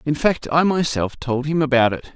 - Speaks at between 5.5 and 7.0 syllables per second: No, 5.0 syllables/s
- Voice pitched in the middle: Yes, medium, 145 Hz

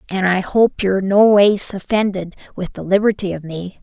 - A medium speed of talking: Yes, average, 170 wpm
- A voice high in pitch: Yes, high, 195 Hz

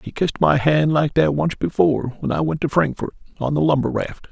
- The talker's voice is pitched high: No, medium, 140 Hz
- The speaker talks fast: Yes, fast, 235 wpm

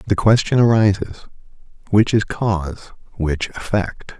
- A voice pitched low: Yes, low, 100 Hz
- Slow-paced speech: Yes, slow, 115 wpm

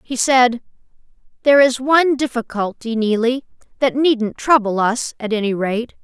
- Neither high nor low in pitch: No, high, 240 Hz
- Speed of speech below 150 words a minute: Yes, average, 140 wpm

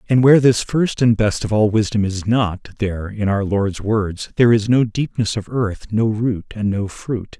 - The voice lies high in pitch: No, low, 110 Hz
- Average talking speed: No, fast, 220 wpm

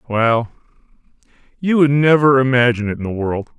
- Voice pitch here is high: No, low, 125 Hz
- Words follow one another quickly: No, average, 150 wpm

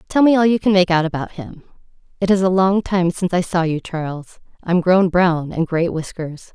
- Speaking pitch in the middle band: Yes, medium, 175 Hz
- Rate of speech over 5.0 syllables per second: Yes, 5.3 syllables/s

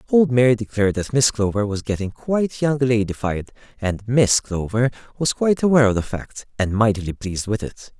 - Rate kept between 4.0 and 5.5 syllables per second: No, 5.7 syllables/s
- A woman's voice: No, male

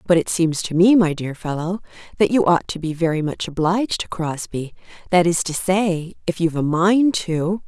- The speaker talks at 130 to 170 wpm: No, fast, 205 wpm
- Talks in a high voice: No, medium, 175 Hz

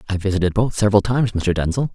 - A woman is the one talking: No, male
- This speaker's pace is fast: Yes, fast, 215 wpm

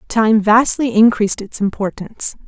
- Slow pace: Yes, slow, 120 wpm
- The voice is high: Yes, high, 215 Hz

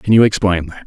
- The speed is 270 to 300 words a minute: Yes, fast, 275 wpm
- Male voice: Yes, male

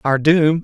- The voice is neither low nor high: Yes, medium, 150 Hz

